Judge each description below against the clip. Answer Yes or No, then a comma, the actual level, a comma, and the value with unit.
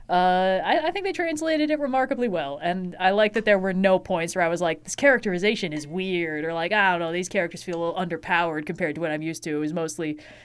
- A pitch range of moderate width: Yes, average, 4.1 semitones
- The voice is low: No, medium, 180 Hz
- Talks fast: Yes, fast, 260 wpm